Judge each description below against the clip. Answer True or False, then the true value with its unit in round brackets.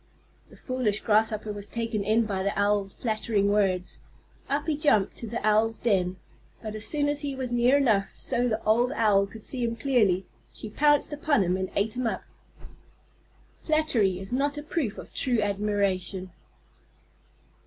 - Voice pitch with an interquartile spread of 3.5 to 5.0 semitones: True (3.9 semitones)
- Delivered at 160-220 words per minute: True (170 wpm)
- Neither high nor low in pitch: False (220 Hz)